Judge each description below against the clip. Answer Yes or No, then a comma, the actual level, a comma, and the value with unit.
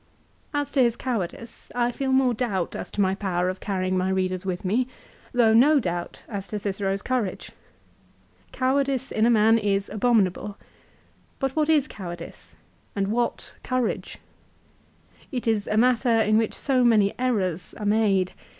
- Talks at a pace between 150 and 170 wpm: Yes, average, 160 wpm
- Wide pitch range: No, average, 4.4 semitones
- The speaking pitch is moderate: No, high, 220 Hz